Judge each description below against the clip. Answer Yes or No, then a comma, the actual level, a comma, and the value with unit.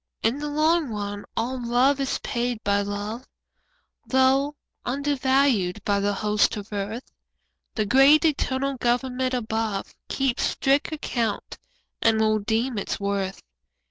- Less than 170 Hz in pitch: No, high, 240 Hz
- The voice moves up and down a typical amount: Yes, average, 4.4 semitones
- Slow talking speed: Yes, slow, 130 wpm